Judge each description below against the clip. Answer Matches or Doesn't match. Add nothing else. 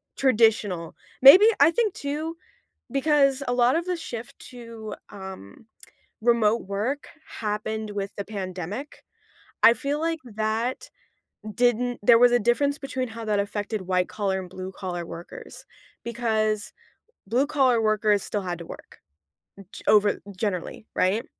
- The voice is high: Matches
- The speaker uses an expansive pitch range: Doesn't match